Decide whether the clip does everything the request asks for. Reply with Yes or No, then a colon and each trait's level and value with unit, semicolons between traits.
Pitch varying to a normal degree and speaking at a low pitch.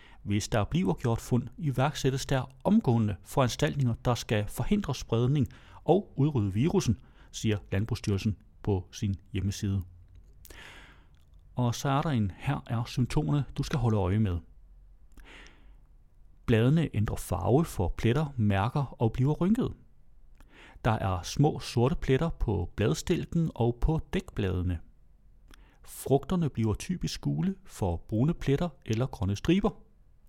No: wide, 6.1 semitones; low, 120 Hz